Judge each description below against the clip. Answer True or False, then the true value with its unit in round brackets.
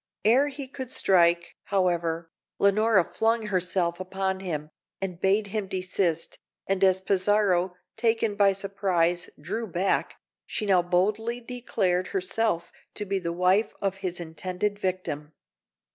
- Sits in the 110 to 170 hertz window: False (190 Hz)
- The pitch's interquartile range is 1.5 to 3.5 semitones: True (2.8 semitones)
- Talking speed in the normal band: False (130 wpm)